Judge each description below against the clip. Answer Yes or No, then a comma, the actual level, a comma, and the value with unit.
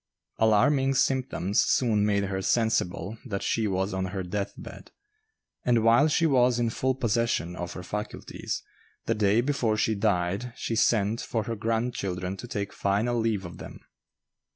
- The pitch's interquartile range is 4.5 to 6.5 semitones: No, average, 3.4 semitones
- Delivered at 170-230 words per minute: No, average, 160 wpm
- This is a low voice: Yes, low, 110 Hz